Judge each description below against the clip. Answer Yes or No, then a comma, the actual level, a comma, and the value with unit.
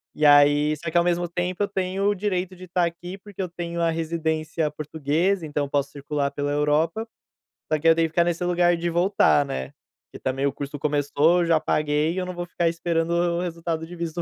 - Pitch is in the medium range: Yes, medium, 165 Hz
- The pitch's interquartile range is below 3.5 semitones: Yes, average, 2.8 semitones